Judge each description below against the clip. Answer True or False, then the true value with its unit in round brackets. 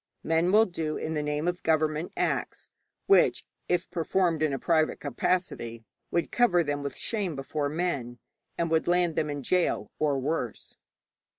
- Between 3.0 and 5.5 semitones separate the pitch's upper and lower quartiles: True (3.3 semitones)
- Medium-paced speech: True (170 wpm)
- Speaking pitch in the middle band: True (160 Hz)